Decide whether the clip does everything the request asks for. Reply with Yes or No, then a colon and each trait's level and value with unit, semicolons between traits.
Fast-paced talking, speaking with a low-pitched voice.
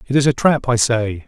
Yes: fast, 280 wpm; low, 125 Hz